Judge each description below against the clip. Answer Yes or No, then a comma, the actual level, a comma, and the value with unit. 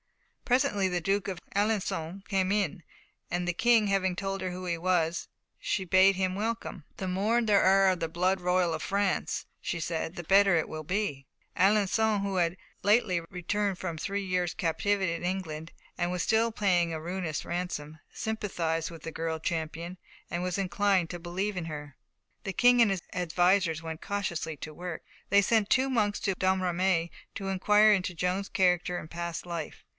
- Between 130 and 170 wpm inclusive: No, average, 180 wpm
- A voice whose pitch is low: No, medium, 185 Hz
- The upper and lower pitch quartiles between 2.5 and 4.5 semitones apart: Yes, average, 2.8 semitones